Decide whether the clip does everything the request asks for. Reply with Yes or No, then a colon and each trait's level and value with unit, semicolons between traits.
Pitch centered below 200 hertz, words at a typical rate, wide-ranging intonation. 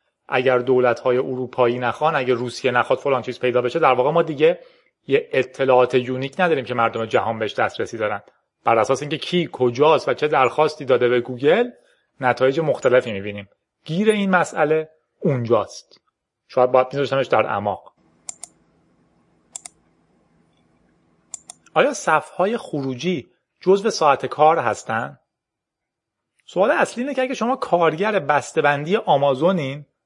Yes: low, 135 Hz; average, 130 wpm; wide, 5.7 semitones